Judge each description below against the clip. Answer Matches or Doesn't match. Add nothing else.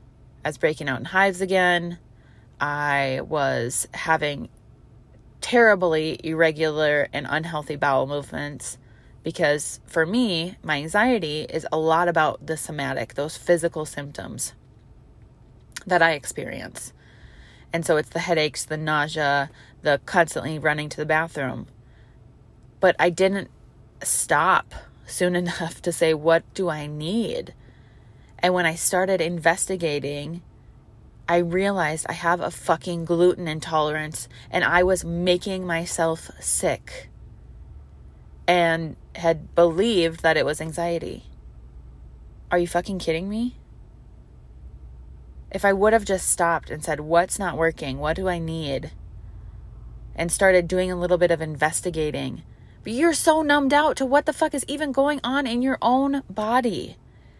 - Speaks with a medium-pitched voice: Matches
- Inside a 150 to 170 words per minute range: Doesn't match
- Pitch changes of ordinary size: Matches